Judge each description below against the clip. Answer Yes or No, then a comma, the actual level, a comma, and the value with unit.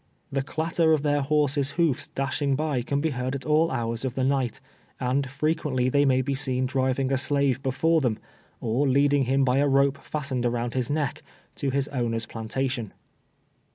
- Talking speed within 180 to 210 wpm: Yes, average, 190 wpm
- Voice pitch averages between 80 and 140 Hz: Yes, low, 135 Hz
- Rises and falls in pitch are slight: Yes, narrow, 2.0 semitones